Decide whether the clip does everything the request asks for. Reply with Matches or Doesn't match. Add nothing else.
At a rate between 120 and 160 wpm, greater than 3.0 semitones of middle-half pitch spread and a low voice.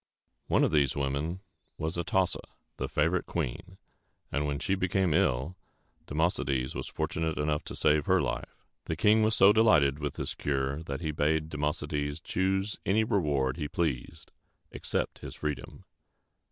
Matches